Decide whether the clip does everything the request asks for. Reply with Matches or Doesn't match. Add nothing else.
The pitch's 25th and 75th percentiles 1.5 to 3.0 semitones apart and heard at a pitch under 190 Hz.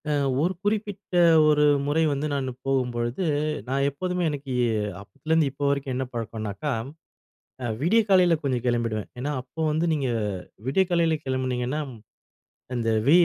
Doesn't match